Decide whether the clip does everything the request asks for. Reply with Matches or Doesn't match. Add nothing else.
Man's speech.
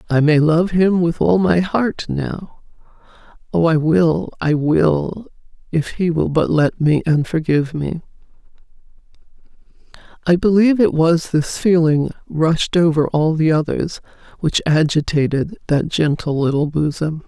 Doesn't match